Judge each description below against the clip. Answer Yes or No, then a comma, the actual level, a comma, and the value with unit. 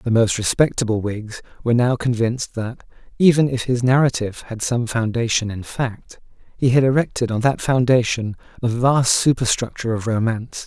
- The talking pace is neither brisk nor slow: Yes, average, 160 wpm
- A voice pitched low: Yes, low, 120 Hz